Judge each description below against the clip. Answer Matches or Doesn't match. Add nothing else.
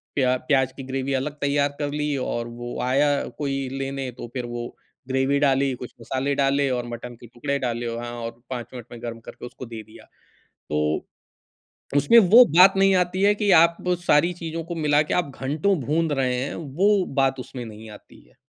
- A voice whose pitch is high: Doesn't match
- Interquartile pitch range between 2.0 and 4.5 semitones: Matches